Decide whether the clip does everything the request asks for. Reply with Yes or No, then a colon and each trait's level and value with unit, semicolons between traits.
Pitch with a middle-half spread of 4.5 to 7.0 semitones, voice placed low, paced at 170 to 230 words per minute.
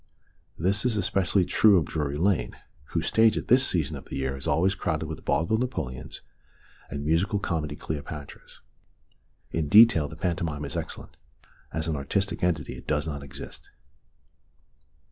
No: average, 5.0 semitones; very low, 80 Hz; average, 155 wpm